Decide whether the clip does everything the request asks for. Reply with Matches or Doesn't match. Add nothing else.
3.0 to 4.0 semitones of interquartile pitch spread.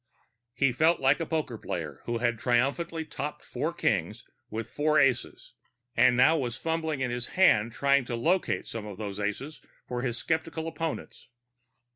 Doesn't match